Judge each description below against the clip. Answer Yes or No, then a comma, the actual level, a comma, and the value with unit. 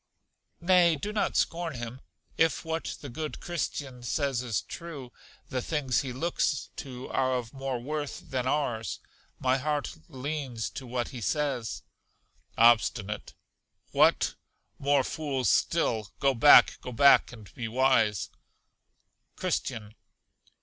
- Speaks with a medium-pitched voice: No, low, 130 Hz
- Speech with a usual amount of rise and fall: Yes, average, 3.6 semitones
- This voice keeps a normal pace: No, slow, 130 wpm